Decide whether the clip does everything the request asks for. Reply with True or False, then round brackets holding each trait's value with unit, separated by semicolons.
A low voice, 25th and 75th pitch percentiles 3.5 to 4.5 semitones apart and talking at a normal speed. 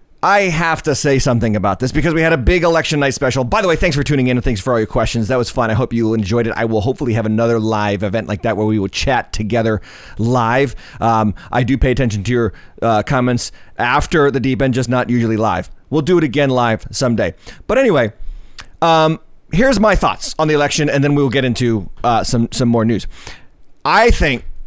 False (125 Hz; 4.1 semitones; 230 wpm)